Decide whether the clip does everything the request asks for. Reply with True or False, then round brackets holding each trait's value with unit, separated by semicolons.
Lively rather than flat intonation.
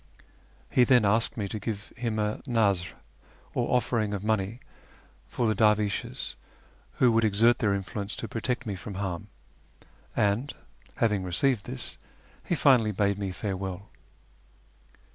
False (2.5 semitones)